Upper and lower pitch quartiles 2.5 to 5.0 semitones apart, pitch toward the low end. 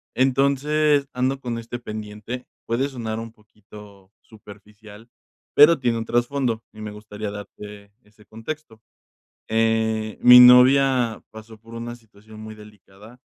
Yes: average, 2.8 semitones; low, 115 Hz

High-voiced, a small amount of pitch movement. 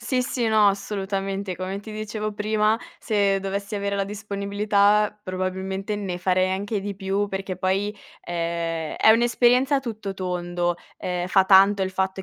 Yes: high, 200 Hz; narrow, 2.0 semitones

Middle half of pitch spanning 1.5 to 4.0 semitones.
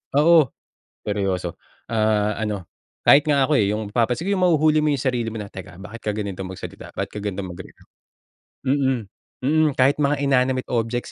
No: wide, 5.4 semitones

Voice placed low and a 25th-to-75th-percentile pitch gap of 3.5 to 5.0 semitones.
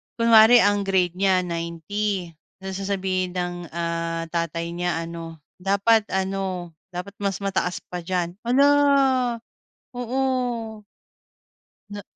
No: high, 190 Hz; average, 4.0 semitones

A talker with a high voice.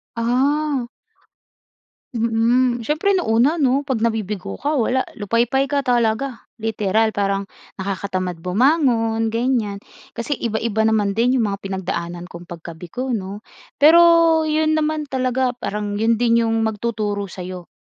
Yes: high, 230 Hz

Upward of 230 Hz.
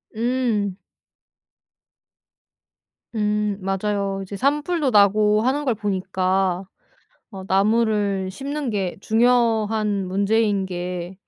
No: high, 210 Hz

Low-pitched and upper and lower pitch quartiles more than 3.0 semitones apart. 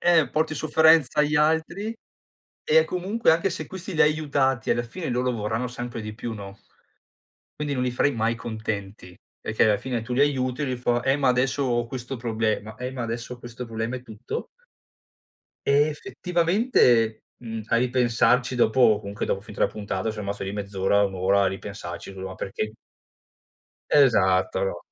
Yes: low, 120 Hz; average, 4.9 semitones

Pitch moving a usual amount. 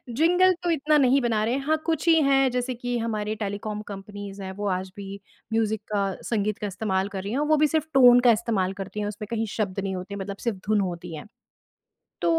Yes: average, 4.3 semitones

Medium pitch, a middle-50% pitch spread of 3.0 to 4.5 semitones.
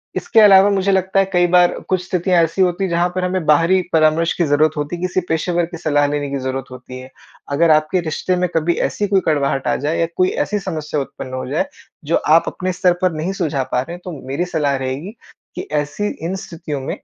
Yes: medium, 170 Hz; average, 3.9 semitones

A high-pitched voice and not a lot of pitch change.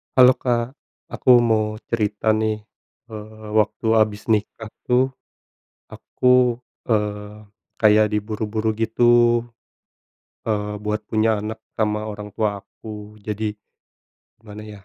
No: low, 110 Hz; narrow, 1.1 semitones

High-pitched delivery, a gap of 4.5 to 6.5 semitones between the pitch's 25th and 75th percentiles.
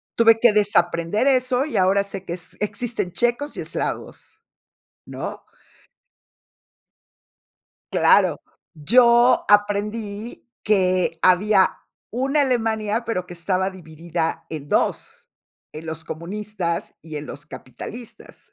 Yes: high, 200 Hz; average, 5.3 semitones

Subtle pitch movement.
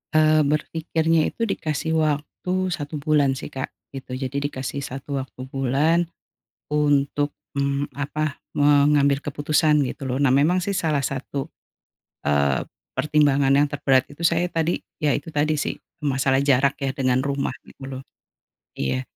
Yes: narrow, 2.0 semitones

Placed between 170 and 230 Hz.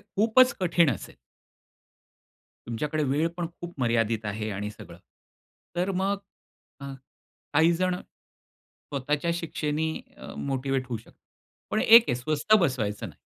No: medium, 150 Hz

